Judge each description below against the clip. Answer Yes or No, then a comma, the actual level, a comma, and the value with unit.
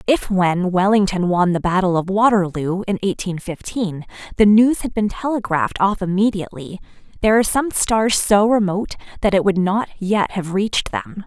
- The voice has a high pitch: Yes, high, 195 Hz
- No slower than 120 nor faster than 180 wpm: Yes, average, 170 wpm